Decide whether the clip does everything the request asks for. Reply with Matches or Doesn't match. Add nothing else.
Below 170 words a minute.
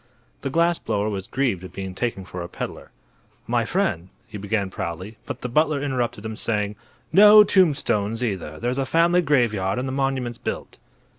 Doesn't match